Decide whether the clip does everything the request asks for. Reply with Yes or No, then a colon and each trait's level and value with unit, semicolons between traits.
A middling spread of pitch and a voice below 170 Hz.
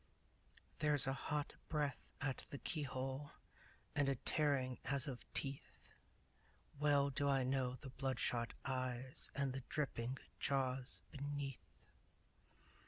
No: narrow, 1.7 semitones; low, 135 Hz